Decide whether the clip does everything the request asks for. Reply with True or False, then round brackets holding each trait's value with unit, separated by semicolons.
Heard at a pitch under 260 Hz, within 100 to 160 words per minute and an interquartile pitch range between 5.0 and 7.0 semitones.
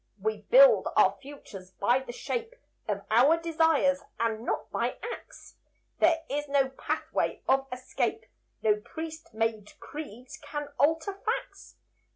False (285 Hz; 135 wpm; 5.5 semitones)